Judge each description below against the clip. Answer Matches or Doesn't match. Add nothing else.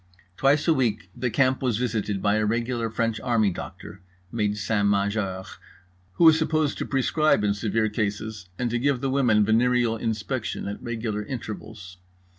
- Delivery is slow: Doesn't match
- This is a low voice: Matches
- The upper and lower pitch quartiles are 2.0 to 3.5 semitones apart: Matches